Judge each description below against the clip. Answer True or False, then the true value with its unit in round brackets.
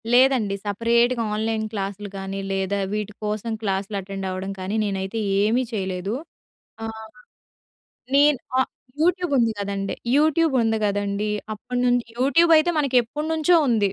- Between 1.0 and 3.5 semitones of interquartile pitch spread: False (4.2 semitones)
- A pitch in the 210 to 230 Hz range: True (220 Hz)